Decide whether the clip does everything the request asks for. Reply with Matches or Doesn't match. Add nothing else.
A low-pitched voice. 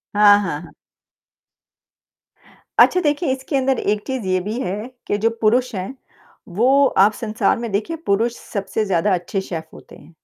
Doesn't match